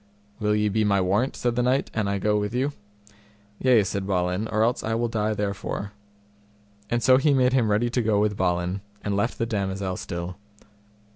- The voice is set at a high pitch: No, low, 105 Hz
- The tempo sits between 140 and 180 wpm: No, average, 200 wpm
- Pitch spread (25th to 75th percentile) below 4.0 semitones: Yes, average, 3.1 semitones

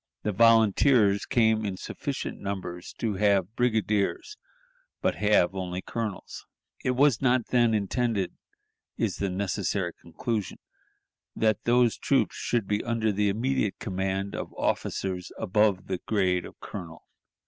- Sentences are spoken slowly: Yes, slow, 130 wpm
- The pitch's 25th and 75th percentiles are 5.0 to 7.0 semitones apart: No, average, 3.1 semitones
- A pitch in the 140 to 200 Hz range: No, low, 105 Hz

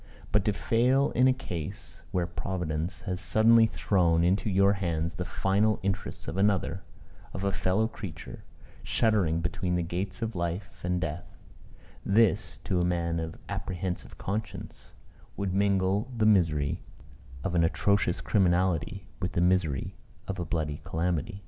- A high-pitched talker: No, very low, 95 Hz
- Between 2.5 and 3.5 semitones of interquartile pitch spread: Yes, average, 2.8 semitones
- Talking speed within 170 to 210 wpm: No, average, 150 wpm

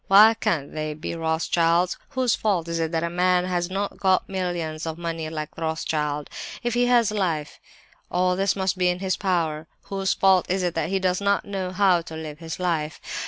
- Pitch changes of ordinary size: Yes, average, 3.0 semitones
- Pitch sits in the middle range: Yes, medium, 180 Hz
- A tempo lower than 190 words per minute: No, fast, 205 wpm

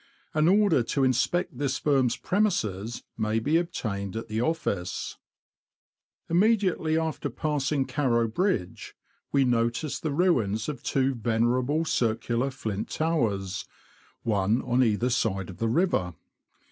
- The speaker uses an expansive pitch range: Yes, wide, 6.0 semitones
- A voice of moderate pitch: No, low, 125 Hz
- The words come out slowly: Yes, slow, 125 wpm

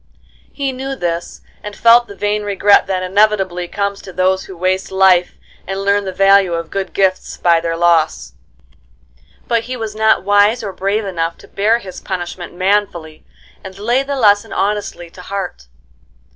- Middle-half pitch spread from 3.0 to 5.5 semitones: No, narrow, 2.5 semitones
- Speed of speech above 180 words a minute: No, average, 170 wpm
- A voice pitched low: No, high, 195 Hz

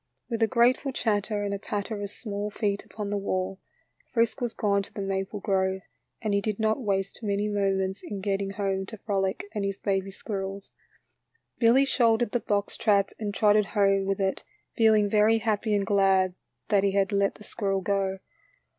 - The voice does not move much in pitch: Yes, narrow, 1.7 semitones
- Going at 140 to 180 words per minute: No, average, 190 wpm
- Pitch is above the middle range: Yes, high, 200 Hz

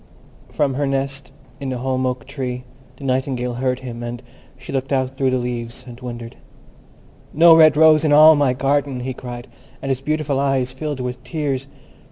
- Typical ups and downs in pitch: No, narrow, 2.0 semitones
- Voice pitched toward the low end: Yes, low, 130 Hz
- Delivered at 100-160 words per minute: No, average, 185 wpm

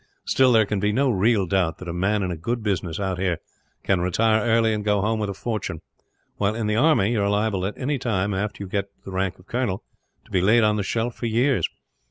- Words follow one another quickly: Yes, fast, 255 wpm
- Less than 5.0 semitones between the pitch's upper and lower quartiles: Yes, average, 3.0 semitones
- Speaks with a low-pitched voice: Yes, low, 105 Hz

